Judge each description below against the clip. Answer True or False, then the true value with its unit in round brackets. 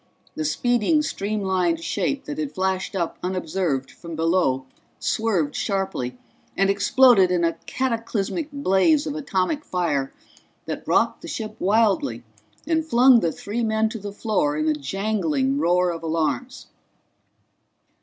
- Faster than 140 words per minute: False (135 wpm)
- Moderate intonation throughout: False (5.7 semitones)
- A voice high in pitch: True (195 Hz)